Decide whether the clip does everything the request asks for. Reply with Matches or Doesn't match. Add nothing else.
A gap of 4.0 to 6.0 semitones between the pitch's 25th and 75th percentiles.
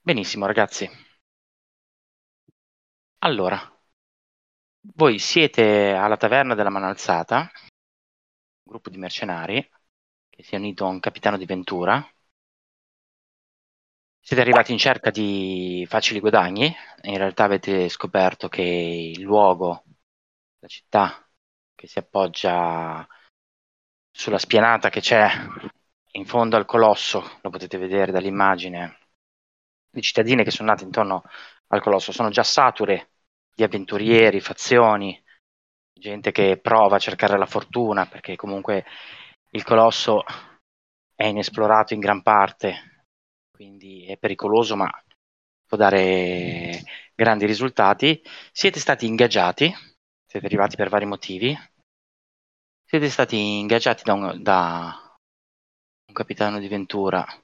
Doesn't match